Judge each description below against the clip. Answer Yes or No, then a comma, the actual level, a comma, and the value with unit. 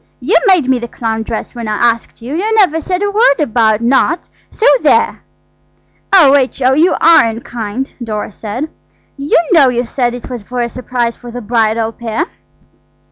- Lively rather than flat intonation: No, average, 4.4 semitones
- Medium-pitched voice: No, high, 245 Hz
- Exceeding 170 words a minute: Yes, average, 180 wpm